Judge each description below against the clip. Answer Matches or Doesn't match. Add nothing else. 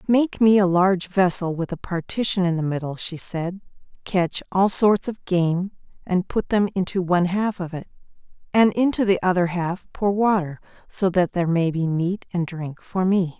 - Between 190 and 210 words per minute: Matches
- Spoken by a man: Doesn't match